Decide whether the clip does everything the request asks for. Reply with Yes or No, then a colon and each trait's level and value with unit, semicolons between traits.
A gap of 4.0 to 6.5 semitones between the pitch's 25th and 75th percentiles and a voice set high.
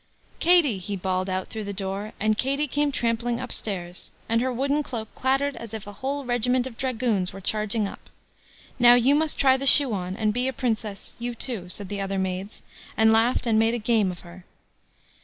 Yes: average, 4.3 semitones; high, 225 Hz